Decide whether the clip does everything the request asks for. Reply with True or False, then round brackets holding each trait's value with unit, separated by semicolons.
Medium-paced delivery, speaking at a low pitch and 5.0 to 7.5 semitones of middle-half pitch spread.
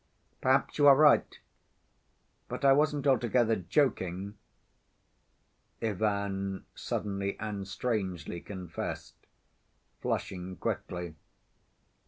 False (80 wpm; 100 Hz; 5.5 semitones)